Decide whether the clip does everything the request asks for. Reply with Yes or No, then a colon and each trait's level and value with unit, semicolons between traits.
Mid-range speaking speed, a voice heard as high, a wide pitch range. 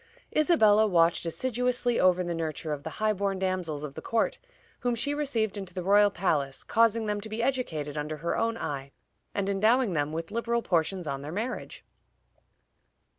Yes: average, 180 wpm; high, 195 Hz; wide, 6.0 semitones